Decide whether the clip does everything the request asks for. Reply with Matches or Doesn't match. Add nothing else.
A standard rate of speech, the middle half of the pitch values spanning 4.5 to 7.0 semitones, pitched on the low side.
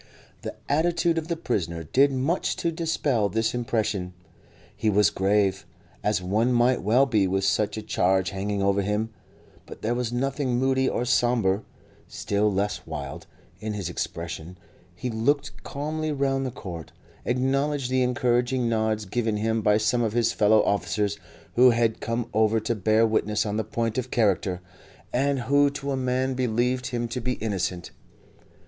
Doesn't match